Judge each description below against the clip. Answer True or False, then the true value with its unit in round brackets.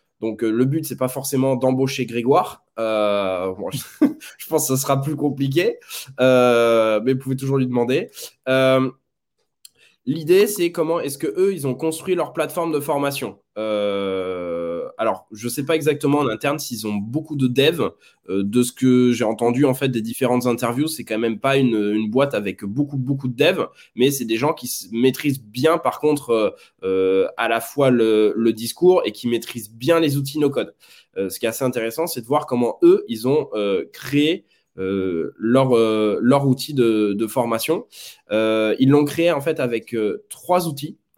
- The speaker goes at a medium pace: True (195 wpm)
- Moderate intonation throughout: True (4.5 semitones)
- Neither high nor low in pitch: False (130 Hz)